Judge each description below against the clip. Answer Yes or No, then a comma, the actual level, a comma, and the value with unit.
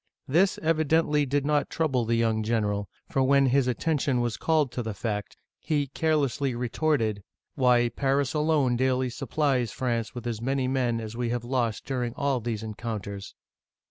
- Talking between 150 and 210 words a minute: Yes, average, 165 wpm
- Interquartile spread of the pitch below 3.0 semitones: No, average, 3.4 semitones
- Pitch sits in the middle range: No, low, 125 Hz